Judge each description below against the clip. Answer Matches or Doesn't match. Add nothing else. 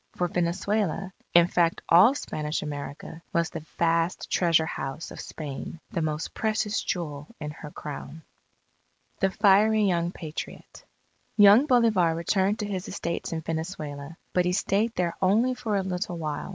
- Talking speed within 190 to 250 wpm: Doesn't match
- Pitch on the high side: Doesn't match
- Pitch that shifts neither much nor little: Matches